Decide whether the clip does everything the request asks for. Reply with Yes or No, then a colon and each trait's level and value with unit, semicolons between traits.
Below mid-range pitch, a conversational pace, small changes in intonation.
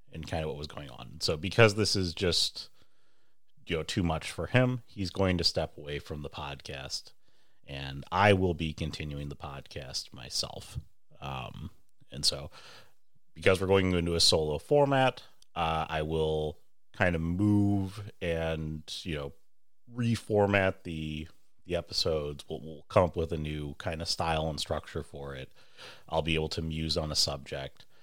No: very low, 80 Hz; average, 170 wpm; average, 3.8 semitones